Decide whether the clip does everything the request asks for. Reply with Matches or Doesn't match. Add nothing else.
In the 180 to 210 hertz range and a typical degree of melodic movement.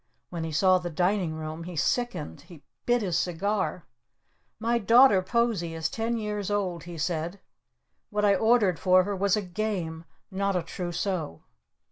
Matches